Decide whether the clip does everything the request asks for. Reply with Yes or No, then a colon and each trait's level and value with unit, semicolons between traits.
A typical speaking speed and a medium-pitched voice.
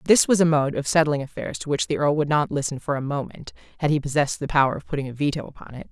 No: fast, 285 wpm; medium, 145 Hz